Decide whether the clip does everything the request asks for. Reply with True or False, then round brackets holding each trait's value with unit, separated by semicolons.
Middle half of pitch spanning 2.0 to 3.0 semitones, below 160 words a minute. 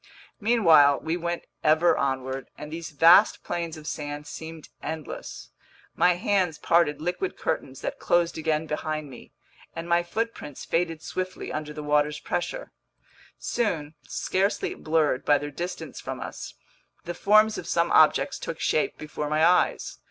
True (2.6 semitones; 150 wpm)